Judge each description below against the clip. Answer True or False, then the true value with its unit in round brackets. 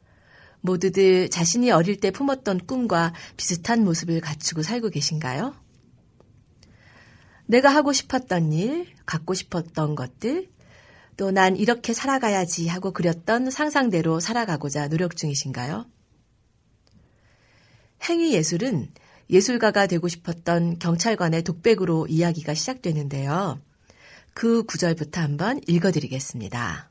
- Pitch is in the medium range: True (170 Hz)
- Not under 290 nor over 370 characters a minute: False (270 characters per minute)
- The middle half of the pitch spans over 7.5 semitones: False (6.2 semitones)